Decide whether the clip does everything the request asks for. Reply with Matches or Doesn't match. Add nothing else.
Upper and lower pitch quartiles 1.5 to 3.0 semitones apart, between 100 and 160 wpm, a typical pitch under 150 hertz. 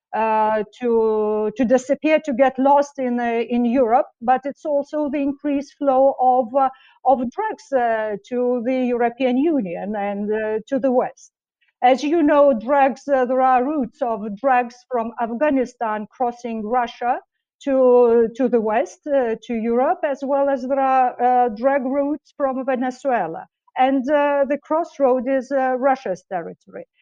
Doesn't match